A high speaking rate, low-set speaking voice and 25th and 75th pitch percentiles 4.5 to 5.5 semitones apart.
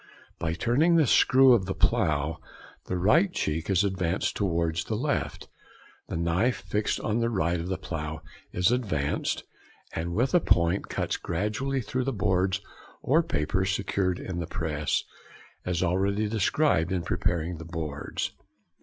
No: average, 155 wpm; very low, 95 Hz; average, 4.8 semitones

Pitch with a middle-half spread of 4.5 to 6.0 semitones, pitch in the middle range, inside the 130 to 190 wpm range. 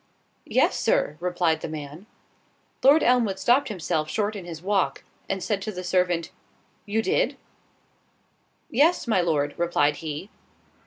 Yes: average, 5.1 semitones; medium, 180 Hz; average, 140 wpm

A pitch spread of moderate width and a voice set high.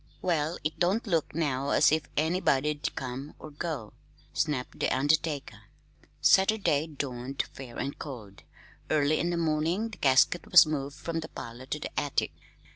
No: average, 3.3 semitones; medium, 150 Hz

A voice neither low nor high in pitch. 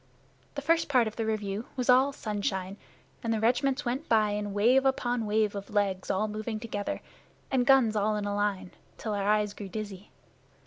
No: high, 215 Hz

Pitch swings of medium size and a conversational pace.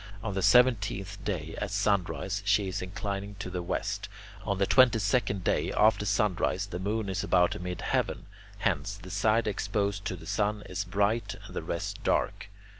No: narrow, 1.9 semitones; average, 180 wpm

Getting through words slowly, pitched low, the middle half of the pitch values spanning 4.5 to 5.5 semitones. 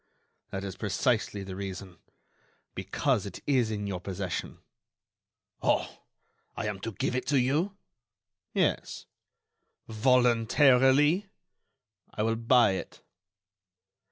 Yes: slow, 100 wpm; low, 115 Hz; average, 4.9 semitones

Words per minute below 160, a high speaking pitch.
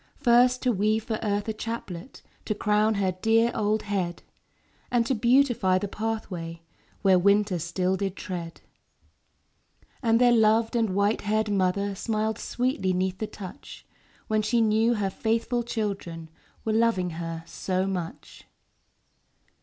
Yes: average, 140 wpm; high, 210 Hz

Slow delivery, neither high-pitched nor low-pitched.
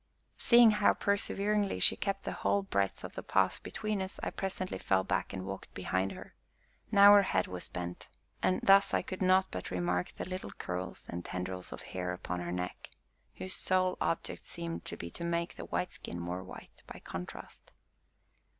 No: average, 185 wpm; medium, 165 Hz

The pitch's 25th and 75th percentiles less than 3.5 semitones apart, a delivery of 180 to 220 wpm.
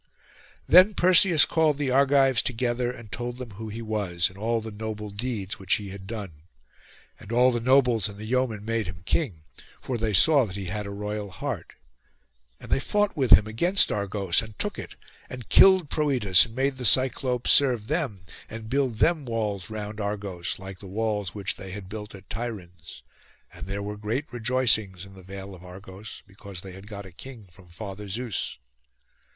No: average, 4.3 semitones; average, 190 wpm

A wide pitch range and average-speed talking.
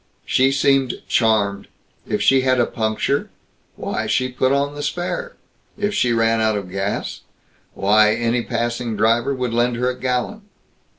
No: average, 3.4 semitones; average, 160 wpm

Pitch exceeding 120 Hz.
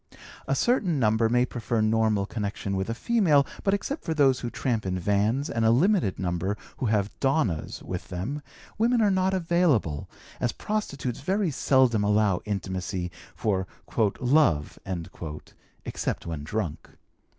No: low, 115 Hz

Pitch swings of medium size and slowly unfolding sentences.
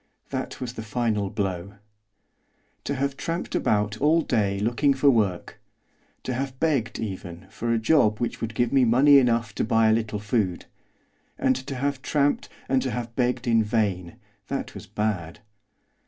No: average, 3.9 semitones; average, 170 wpm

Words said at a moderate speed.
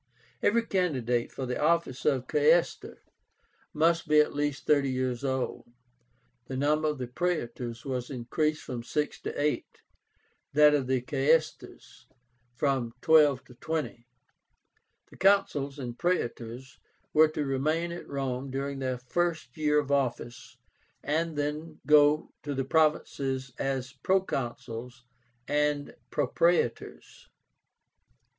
No: slow, 120 wpm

